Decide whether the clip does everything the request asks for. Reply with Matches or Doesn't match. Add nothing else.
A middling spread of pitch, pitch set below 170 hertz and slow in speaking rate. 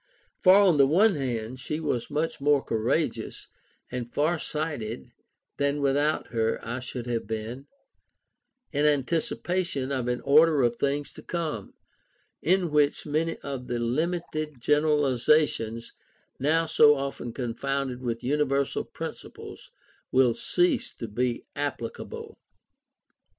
Matches